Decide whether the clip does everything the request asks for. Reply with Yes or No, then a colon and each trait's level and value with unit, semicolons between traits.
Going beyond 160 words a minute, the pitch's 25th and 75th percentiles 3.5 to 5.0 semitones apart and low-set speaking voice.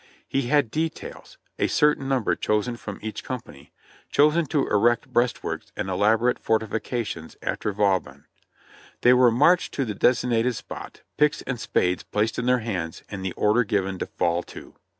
Yes: average, 170 wpm; average, 3.9 semitones; low, 115 Hz